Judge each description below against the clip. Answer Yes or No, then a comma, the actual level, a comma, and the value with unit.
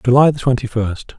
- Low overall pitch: Yes, low, 125 Hz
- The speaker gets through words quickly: No, average, 150 wpm